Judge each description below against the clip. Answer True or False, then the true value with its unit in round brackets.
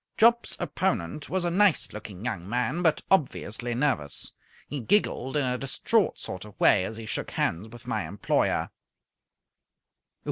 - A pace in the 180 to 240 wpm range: False (150 wpm)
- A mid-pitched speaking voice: False (125 Hz)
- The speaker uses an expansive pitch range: True (8.4 semitones)